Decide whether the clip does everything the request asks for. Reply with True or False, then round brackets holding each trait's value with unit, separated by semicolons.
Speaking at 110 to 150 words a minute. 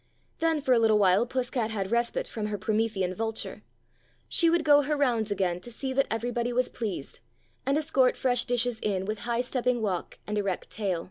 False (200 wpm)